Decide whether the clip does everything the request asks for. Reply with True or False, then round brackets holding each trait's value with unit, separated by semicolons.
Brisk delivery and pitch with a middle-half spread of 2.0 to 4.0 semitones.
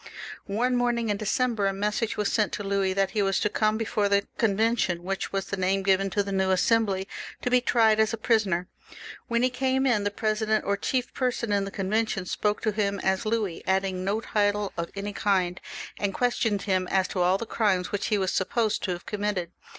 True (215 wpm; 2.4 semitones)